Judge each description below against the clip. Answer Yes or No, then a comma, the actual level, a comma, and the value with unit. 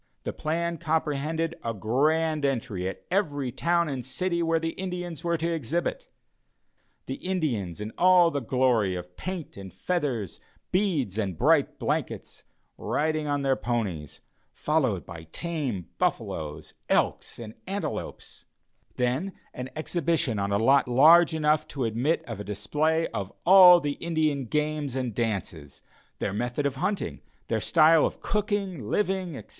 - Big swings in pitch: Yes, wide, 6.5 semitones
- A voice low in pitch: No, medium, 145 Hz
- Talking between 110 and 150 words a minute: Yes, average, 145 wpm